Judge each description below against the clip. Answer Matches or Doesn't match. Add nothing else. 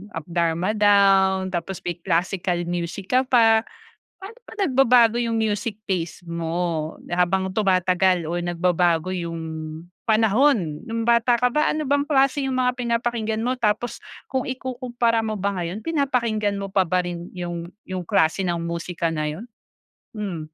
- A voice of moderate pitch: Doesn't match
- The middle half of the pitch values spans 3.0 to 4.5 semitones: Doesn't match